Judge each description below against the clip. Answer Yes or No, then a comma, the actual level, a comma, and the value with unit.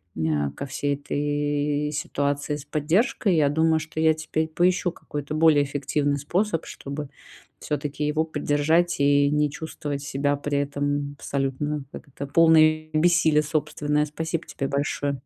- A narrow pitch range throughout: Yes, narrow, 1.7 semitones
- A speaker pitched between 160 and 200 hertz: No, medium, 150 Hz